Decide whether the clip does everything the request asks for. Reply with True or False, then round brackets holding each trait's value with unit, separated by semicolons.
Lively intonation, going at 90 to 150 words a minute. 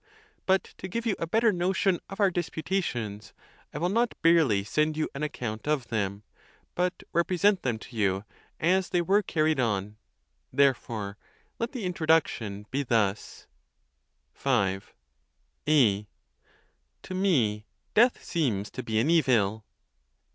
True (9.0 semitones; 140 wpm)